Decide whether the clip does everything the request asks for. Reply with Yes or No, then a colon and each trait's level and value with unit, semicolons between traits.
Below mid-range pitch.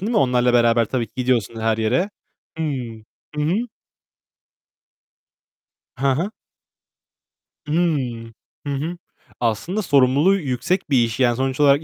Yes: low, 130 Hz